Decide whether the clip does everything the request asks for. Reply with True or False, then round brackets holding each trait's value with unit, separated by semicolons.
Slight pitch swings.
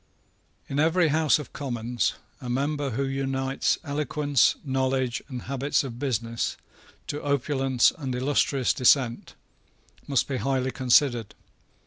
True (2.3 semitones)